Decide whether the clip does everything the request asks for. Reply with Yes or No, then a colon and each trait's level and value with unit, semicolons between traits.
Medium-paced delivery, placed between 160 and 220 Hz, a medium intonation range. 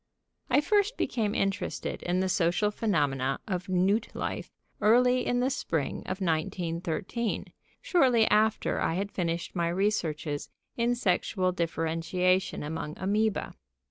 No: slow, 130 wpm; medium, 185 Hz; average, 4.8 semitones